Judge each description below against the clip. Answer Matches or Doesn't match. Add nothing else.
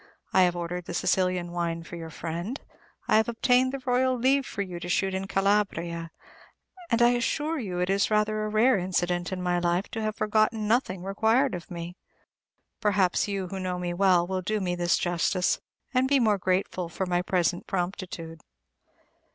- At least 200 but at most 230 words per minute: Doesn't match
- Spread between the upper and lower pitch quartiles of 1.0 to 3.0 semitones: Doesn't match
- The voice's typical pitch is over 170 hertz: Matches